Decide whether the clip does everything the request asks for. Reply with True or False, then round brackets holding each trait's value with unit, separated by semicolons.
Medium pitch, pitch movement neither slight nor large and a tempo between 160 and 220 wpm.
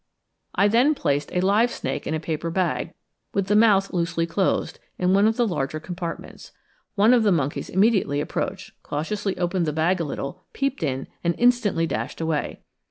True (180 Hz; 4.3 semitones; 180 wpm)